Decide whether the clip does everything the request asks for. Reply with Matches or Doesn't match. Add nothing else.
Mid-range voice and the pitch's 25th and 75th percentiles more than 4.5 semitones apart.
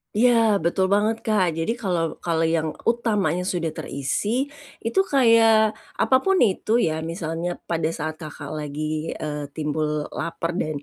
Matches